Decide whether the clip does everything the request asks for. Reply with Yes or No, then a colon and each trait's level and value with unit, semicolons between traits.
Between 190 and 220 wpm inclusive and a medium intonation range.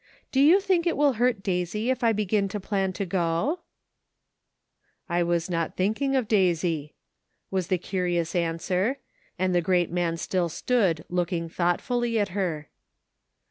No: average, 170 wpm; average, 4.5 semitones